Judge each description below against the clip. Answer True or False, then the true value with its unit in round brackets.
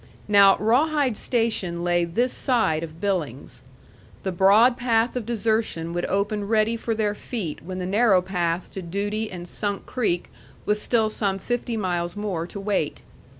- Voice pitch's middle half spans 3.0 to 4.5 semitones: True (4.1 semitones)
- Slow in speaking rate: False (160 wpm)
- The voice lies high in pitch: True (205 Hz)